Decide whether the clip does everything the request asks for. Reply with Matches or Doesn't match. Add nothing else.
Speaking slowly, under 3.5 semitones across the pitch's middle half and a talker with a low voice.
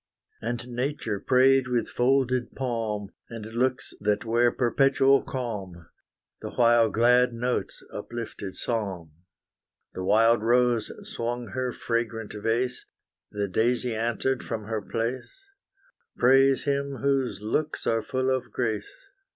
Matches